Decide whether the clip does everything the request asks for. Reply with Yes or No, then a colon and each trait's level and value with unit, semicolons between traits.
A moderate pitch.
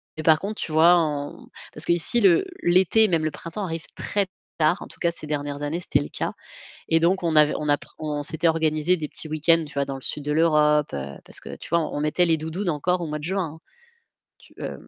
Yes: medium, 160 Hz